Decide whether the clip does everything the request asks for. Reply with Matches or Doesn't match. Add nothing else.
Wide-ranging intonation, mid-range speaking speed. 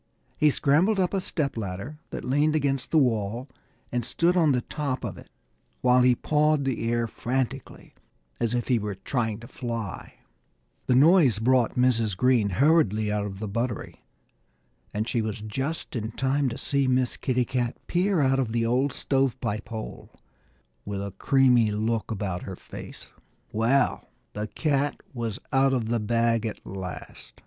Doesn't match